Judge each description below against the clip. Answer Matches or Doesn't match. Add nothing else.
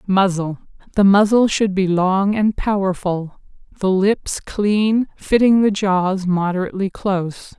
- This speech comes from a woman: Matches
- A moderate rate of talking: Doesn't match